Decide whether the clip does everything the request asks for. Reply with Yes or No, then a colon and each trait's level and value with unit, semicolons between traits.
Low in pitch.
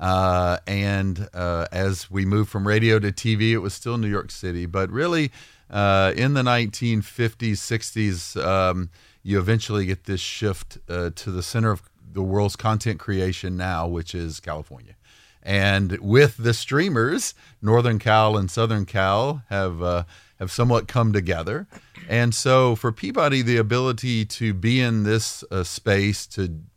Yes: low, 105 Hz